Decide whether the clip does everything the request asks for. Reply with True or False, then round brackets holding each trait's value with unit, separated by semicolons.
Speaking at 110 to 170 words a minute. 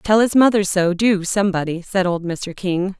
False (200 wpm)